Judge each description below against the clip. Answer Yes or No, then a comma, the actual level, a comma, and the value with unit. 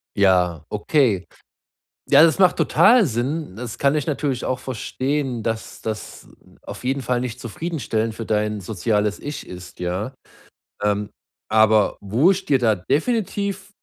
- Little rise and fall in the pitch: No, wide, 5.7 semitones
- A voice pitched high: No, low, 120 Hz